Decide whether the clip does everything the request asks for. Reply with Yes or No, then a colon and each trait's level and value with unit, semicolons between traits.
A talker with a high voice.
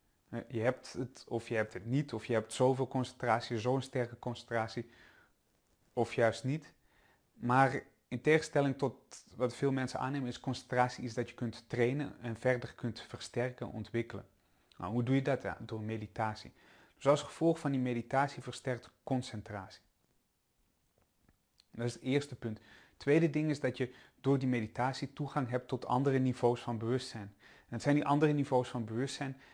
No: low, 125 Hz